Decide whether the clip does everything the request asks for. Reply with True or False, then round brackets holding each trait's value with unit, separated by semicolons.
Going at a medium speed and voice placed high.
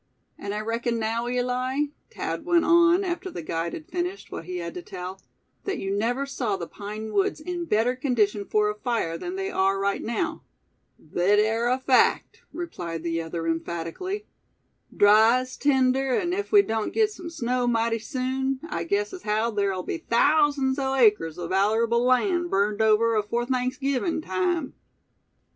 True (170 wpm; 240 Hz)